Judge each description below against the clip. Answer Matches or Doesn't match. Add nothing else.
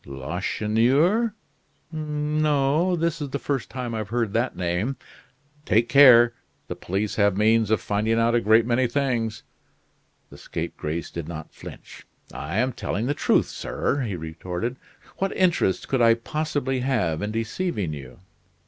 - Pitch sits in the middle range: Doesn't match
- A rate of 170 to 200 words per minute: Doesn't match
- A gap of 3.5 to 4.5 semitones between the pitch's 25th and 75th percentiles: Doesn't match